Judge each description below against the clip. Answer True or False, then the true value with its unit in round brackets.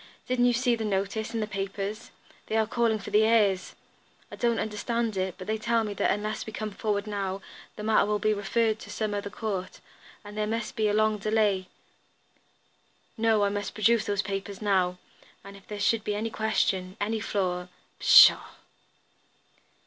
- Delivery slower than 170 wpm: False (190 wpm)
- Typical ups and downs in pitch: False (1.8 semitones)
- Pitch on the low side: False (210 Hz)